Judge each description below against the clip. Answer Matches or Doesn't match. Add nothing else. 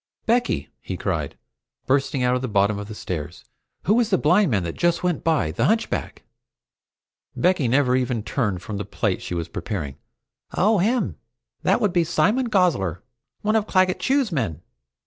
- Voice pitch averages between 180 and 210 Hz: Doesn't match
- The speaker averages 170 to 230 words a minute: Matches